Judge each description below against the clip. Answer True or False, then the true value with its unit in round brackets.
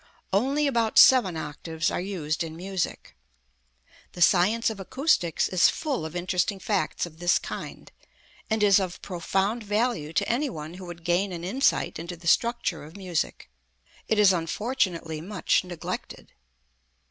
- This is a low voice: False (185 Hz)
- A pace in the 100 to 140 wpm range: False (150 wpm)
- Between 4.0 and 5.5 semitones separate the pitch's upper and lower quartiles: True (4.3 semitones)